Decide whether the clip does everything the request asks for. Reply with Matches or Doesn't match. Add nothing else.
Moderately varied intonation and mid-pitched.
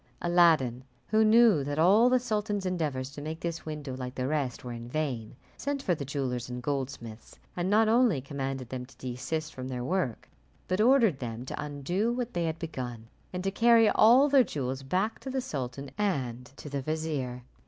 Doesn't match